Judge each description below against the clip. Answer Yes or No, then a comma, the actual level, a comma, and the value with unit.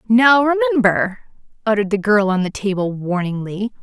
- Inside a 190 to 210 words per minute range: No, average, 140 wpm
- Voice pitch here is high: Yes, high, 215 Hz